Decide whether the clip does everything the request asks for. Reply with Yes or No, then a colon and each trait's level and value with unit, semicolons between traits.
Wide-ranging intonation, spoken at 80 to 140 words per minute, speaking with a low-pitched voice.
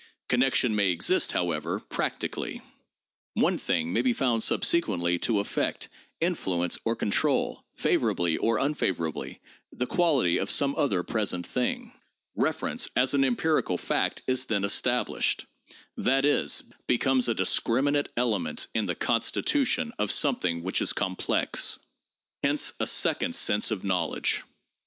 Yes: wide, 7.0 semitones; slow, 135 wpm; low, 115 Hz